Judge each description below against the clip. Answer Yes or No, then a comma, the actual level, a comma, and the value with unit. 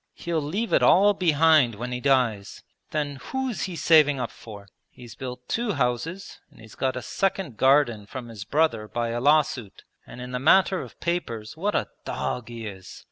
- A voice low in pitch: Yes, low, 130 Hz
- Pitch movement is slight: No, wide, 5.6 semitones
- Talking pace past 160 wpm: Yes, average, 190 wpm